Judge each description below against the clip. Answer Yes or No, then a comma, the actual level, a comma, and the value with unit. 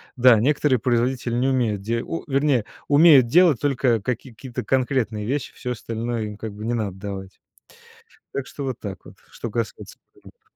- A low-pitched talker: Yes, low, 120 Hz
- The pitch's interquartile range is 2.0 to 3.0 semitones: No, average, 3.4 semitones